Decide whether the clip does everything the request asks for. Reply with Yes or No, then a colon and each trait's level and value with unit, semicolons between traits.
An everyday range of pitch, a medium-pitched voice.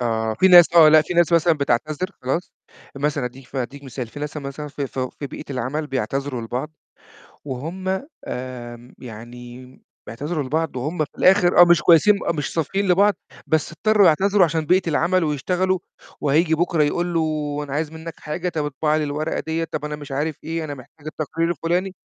Yes: average, 3.9 semitones; medium, 155 Hz